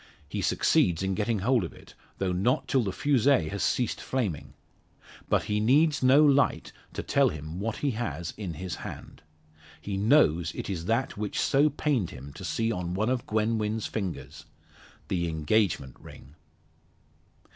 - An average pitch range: No, wide, 6.1 semitones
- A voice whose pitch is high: No, low, 105 Hz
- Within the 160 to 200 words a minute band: Yes, average, 165 wpm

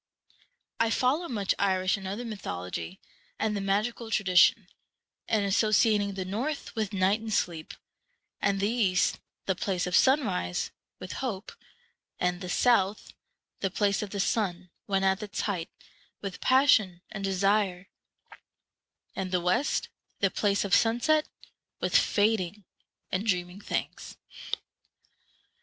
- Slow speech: Yes, slow, 130 wpm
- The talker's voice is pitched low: No, high, 200 Hz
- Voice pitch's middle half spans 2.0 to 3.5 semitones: Yes, average, 2.9 semitones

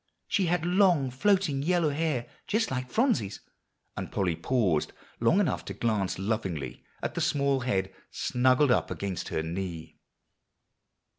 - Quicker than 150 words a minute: No, average, 140 wpm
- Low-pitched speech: Yes, low, 130 Hz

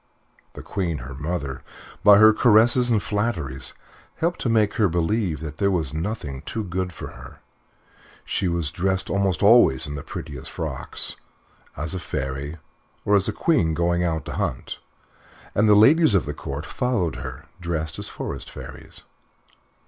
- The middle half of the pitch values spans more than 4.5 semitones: Yes, wide, 5.6 semitones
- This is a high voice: No, very low, 90 Hz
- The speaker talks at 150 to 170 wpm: Yes, average, 165 wpm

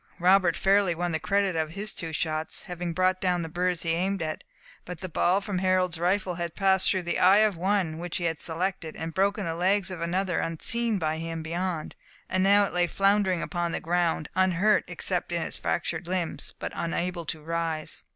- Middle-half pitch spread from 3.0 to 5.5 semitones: No, narrow, 2.4 semitones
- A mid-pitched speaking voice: Yes, medium, 180 Hz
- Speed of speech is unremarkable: No, fast, 210 wpm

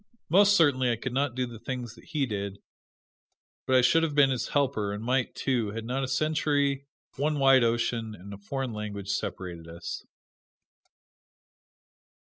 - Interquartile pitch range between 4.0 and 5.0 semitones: Yes, average, 4.4 semitones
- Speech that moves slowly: No, average, 165 wpm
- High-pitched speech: No, low, 125 Hz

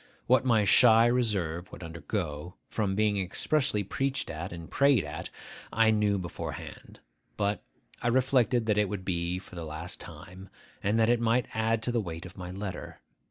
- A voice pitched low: Yes, low, 100 Hz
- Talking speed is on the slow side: No, average, 175 wpm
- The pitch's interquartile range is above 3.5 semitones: Yes, average, 4.5 semitones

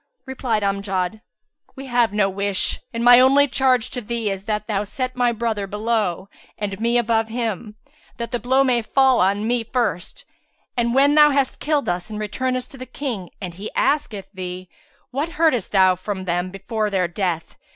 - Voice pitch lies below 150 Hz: No, high, 225 Hz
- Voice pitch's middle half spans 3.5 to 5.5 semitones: Yes, average, 4.4 semitones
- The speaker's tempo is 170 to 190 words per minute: Yes, average, 185 wpm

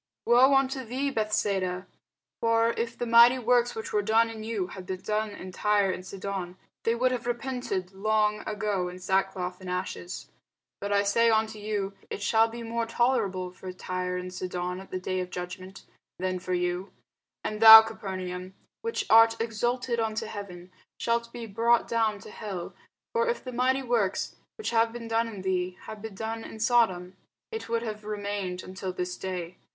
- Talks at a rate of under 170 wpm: No, average, 180 wpm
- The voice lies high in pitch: Yes, high, 210 Hz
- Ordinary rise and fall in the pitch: Yes, average, 3.8 semitones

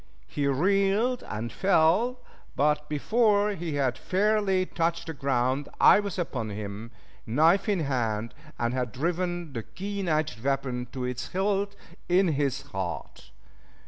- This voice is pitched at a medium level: Yes, medium, 155 Hz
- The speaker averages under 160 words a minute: Yes, average, 140 wpm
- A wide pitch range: Yes, wide, 7.3 semitones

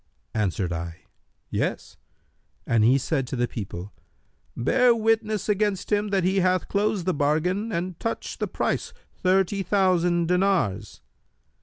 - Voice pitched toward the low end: No, medium, 180 Hz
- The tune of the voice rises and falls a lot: Yes, wide, 7.5 semitones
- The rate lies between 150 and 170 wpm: No, slow, 135 wpm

